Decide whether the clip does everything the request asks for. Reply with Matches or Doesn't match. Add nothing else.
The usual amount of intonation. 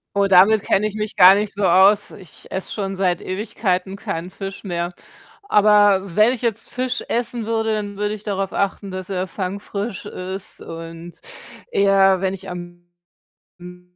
Doesn't match